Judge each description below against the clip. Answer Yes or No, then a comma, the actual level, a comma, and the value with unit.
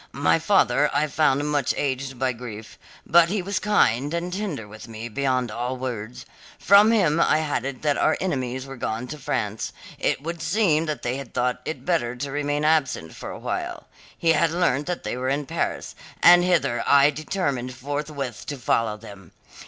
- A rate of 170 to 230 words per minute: Yes, average, 185 wpm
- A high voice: No, medium, 140 Hz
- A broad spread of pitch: No, average, 4.3 semitones